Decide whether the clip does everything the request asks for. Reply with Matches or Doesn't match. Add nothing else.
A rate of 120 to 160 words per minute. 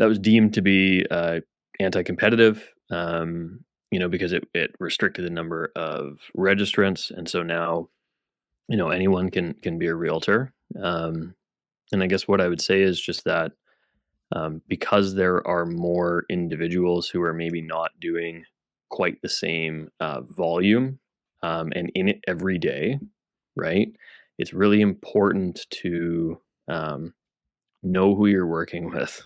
Matches